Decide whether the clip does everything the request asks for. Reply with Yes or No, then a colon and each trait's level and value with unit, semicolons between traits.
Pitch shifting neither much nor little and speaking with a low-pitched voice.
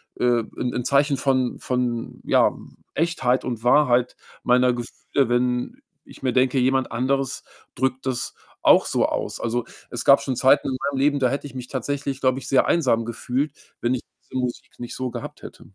No: narrow, 1.9 semitones; low, 130 Hz